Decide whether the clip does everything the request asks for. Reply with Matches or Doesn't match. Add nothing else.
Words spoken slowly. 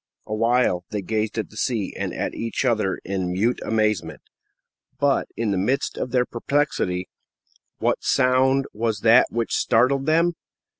Doesn't match